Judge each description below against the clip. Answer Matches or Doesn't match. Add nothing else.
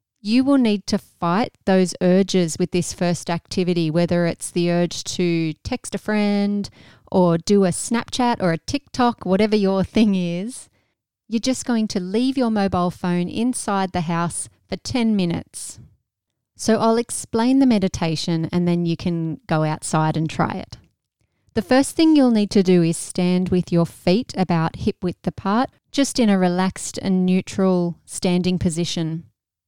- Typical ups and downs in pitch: Matches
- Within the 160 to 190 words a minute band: Matches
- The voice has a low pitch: Doesn't match